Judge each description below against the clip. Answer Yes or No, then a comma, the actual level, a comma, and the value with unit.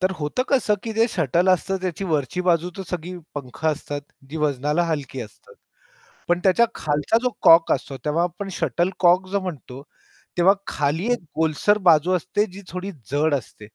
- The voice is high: No, medium, 175 Hz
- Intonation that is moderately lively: Yes, average, 4.2 semitones